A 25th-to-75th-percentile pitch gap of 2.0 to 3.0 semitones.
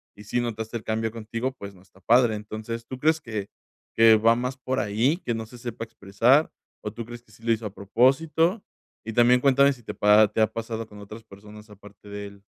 Yes: narrow, 2.6 semitones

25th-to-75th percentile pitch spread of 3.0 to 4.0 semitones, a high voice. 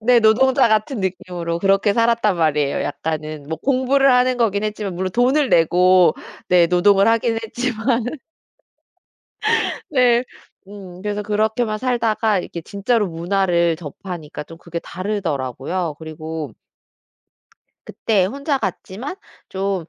No: average, 5.1 semitones; high, 200 Hz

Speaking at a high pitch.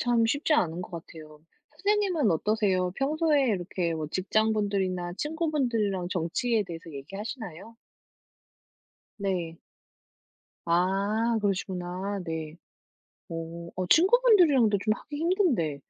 Yes: high, 200 Hz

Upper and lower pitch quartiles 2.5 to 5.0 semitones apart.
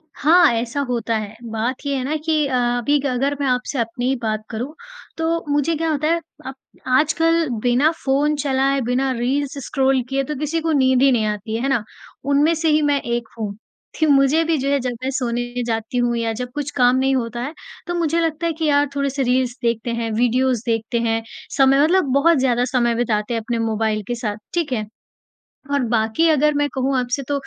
Yes: average, 3.6 semitones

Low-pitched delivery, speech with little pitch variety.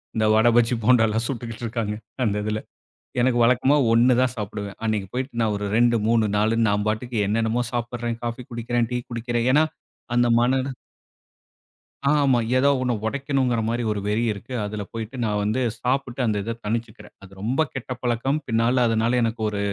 Yes: low, 115 Hz; narrow, 2.2 semitones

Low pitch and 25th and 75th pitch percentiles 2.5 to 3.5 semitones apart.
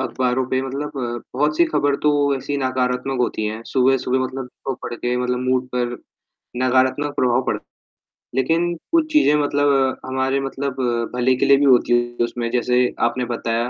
No: low, 130 Hz; narrow, 1.9 semitones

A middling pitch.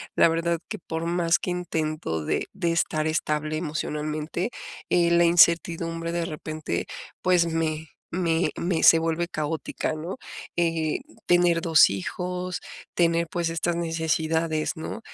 Yes: medium, 165 Hz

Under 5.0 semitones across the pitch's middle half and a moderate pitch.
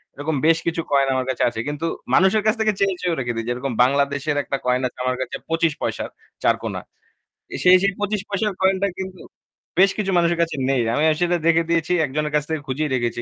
No: average, 5.3 semitones; medium, 160 Hz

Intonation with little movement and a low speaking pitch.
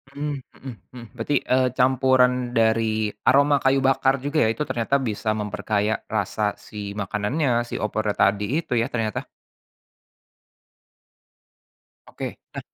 No: average, 3.7 semitones; low, 120 Hz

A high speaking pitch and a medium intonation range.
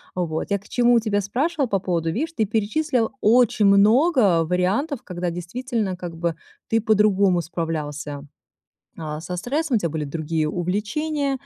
No: high, 200 Hz; wide, 6.1 semitones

